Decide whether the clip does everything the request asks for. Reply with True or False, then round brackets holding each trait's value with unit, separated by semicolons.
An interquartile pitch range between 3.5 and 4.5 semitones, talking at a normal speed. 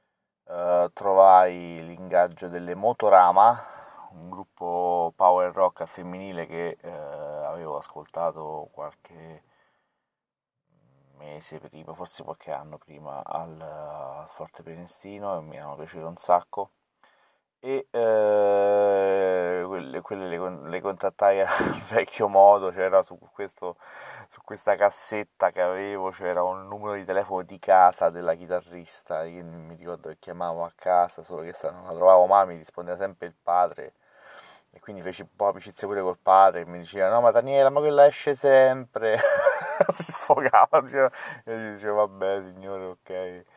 False (2.5 semitones; 145 wpm)